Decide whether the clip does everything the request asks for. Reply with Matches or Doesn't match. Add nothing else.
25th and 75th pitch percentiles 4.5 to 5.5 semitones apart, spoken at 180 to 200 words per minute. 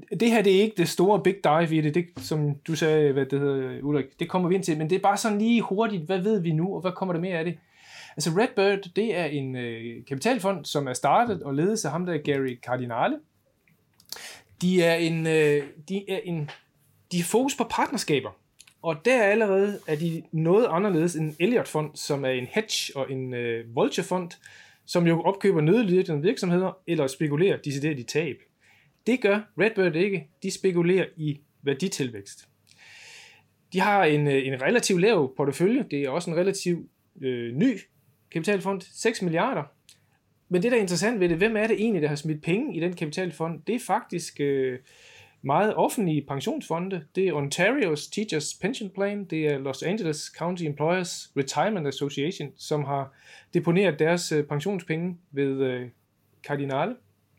Matches